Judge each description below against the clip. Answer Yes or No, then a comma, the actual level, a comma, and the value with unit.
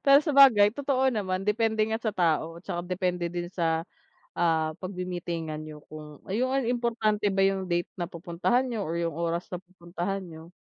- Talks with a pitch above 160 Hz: Yes, medium, 185 Hz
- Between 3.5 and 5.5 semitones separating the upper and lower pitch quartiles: Yes, average, 4.5 semitones